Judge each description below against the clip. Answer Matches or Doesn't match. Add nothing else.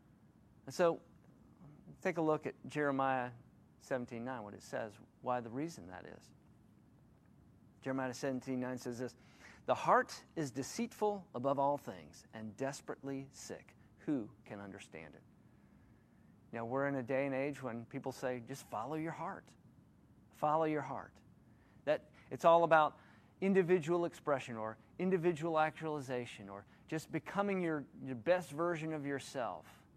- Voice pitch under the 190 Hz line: Matches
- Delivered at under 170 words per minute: Matches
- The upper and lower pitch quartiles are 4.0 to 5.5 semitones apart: Matches